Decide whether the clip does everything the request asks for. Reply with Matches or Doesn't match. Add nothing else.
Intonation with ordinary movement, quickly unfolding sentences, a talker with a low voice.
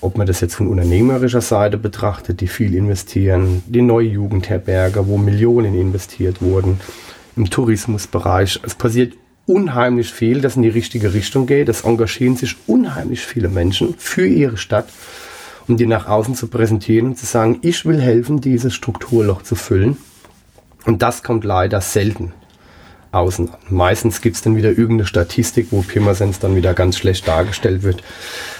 Doesn't match